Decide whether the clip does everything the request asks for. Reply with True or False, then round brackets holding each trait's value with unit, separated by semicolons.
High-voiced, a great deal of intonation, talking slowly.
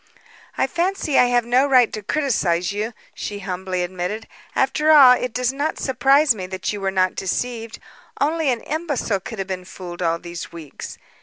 False (225 Hz; 6.3 semitones; 180 wpm)